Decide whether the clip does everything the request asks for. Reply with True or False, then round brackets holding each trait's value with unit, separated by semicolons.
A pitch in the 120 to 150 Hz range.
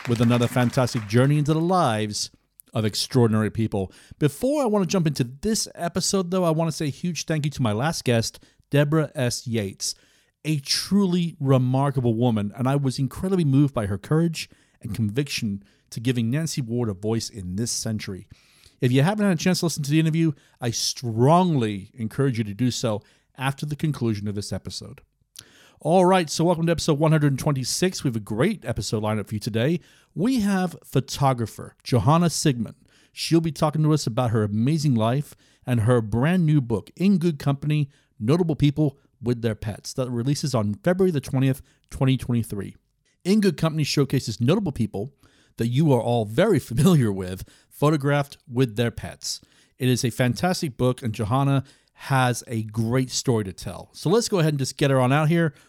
True (135 Hz)